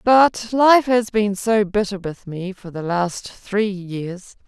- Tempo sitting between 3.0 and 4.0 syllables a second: Yes, 3.3 syllables/s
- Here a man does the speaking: No, female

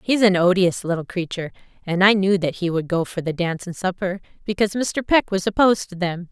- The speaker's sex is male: No, female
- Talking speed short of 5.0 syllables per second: No, 6.1 syllables/s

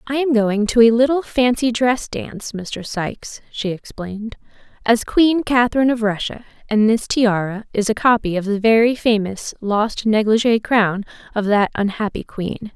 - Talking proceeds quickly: No, average, 165 wpm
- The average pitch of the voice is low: No, high, 225 Hz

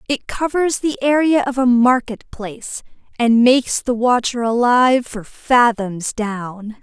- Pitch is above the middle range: Yes, high, 245 Hz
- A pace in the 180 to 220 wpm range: No, average, 140 wpm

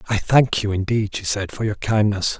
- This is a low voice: Yes, low, 105 Hz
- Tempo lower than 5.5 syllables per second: Yes, 5.0 syllables/s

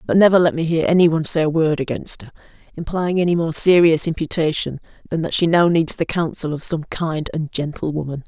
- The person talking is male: No, female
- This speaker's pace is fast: Yes, fast, 220 wpm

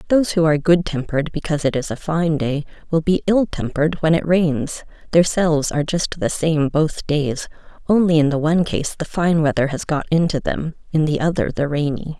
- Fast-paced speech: Yes, fast, 210 wpm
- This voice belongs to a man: No, female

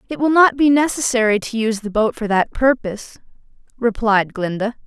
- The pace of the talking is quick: No, average, 175 wpm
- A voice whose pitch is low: No, high, 230 Hz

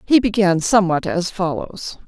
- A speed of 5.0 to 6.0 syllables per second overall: No, 4.8 syllables/s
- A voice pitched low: No, high, 190 Hz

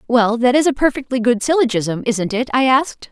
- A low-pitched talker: No, high, 245 Hz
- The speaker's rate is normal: No, fast, 210 wpm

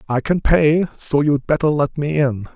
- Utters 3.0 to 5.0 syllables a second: Yes, 4.5 syllables/s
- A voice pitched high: No, medium, 145 Hz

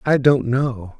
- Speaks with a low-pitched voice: Yes, low, 130 Hz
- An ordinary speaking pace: Yes, average, 180 wpm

